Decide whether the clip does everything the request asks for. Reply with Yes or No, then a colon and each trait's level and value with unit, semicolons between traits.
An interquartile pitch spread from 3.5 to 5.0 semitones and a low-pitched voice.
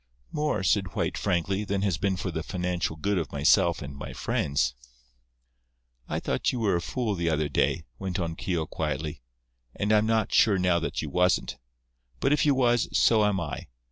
Yes: average, 4.2 semitones; very low, 90 Hz